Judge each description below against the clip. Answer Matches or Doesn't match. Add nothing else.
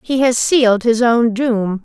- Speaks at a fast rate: Doesn't match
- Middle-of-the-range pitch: Doesn't match